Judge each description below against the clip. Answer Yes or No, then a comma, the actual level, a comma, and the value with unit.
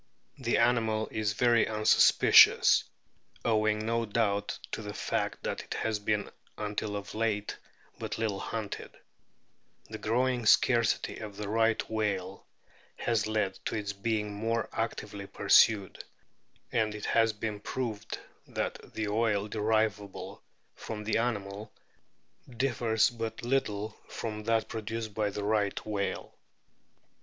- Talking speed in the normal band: No, slow, 130 wpm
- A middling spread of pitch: No, narrow, 1.6 semitones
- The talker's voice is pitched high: No, low, 110 Hz